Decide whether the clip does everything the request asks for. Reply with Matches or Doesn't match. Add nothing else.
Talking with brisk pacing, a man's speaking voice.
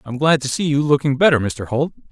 Matches